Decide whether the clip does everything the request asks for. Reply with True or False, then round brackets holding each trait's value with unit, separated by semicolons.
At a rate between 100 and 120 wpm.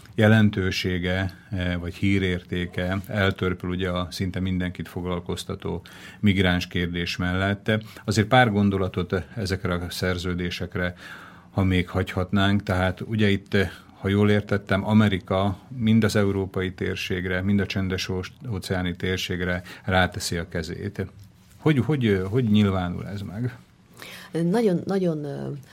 True (110 wpm)